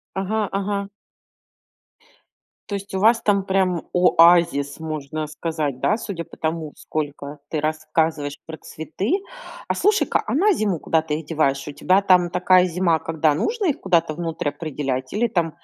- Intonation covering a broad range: No, average, 3.8 semitones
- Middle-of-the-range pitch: Yes, medium, 165 Hz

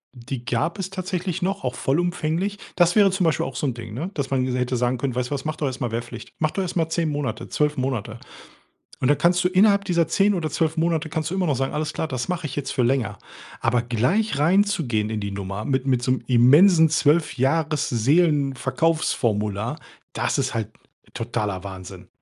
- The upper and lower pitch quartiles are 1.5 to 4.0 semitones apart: No, wide, 5.7 semitones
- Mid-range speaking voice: Yes, medium, 145 Hz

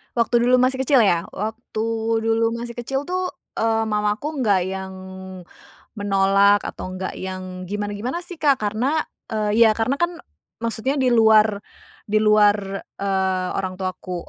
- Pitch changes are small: No, average, 3.6 semitones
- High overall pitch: Yes, high, 215 Hz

